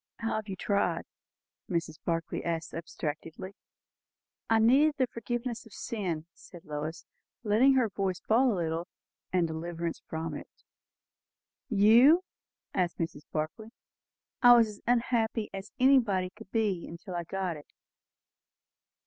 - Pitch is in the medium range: No, high, 195 Hz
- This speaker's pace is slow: Yes, slow, 130 wpm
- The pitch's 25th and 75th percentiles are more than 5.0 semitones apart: Yes, wide, 5.4 semitones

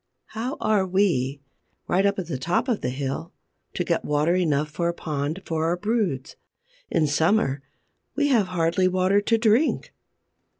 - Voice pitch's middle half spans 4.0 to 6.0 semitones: Yes, average, 5.2 semitones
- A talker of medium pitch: Yes, medium, 175 Hz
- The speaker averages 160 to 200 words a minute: Yes, average, 165 wpm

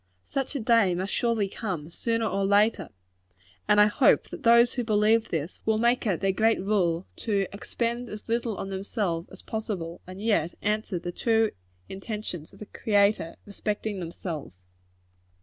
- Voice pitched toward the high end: Yes, high, 210 Hz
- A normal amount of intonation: Yes, average, 3.3 semitones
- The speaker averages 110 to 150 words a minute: No, average, 165 wpm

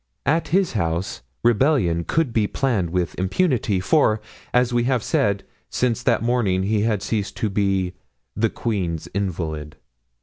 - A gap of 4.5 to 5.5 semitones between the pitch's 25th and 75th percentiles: Yes, average, 4.8 semitones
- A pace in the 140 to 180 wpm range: Yes, average, 145 wpm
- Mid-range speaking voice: No, low, 105 Hz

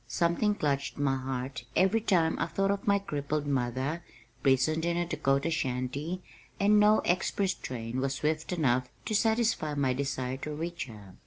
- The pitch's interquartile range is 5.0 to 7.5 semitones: Yes, wide, 5.4 semitones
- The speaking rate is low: No, average, 165 wpm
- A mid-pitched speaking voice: Yes, medium, 150 Hz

